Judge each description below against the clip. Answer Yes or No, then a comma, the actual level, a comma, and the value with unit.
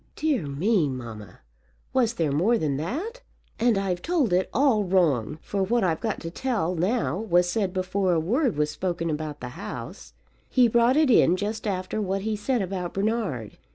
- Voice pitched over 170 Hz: Yes, high, 190 Hz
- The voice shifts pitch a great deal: Yes, wide, 5.8 semitones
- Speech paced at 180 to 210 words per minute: Yes, average, 185 wpm